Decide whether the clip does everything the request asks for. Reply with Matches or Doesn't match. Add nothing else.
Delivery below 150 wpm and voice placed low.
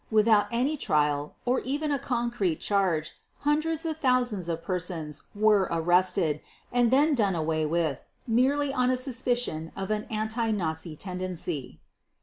Doesn't match